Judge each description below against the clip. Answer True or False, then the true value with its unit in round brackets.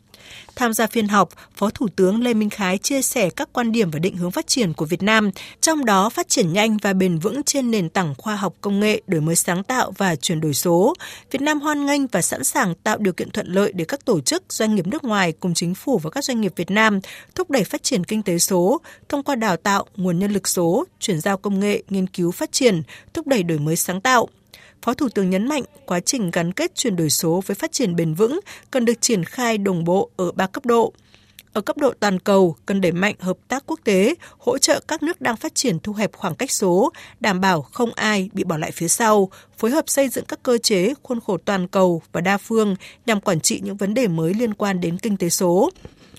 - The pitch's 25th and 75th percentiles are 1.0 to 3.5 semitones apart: False (5.0 semitones)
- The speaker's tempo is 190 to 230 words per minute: False (250 wpm)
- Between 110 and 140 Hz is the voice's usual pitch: False (205 Hz)